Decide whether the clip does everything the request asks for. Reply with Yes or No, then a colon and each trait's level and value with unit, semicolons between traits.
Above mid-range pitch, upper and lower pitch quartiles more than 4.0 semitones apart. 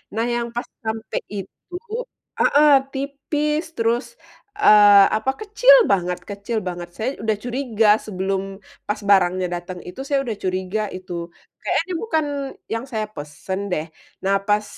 Yes: high, 215 Hz; average, 5.1 semitones